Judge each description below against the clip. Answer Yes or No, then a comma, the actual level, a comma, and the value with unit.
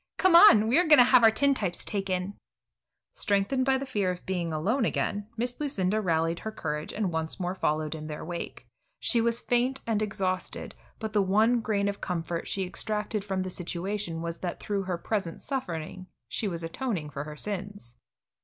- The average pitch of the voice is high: Yes, high, 195 Hz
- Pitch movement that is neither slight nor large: Yes, average, 4.4 semitones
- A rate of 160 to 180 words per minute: No, average, 190 wpm